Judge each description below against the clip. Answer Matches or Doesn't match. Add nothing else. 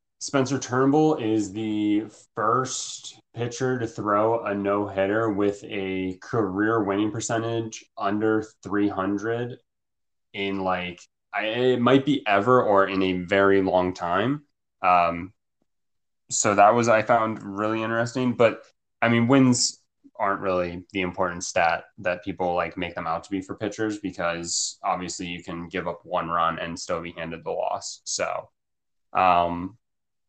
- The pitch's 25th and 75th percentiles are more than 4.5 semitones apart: Doesn't match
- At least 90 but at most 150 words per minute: Matches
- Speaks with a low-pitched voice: Matches